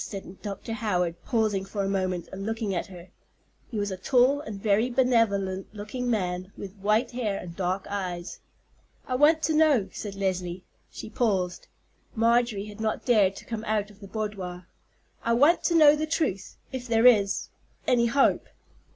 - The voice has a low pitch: No, high, 210 Hz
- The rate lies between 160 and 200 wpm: Yes, average, 165 wpm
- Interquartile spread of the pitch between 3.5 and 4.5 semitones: Yes, average, 3.8 semitones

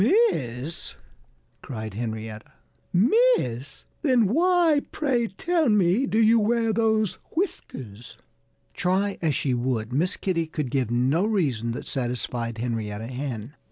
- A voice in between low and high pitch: Yes, medium, 160 Hz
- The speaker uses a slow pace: Yes, slow, 120 wpm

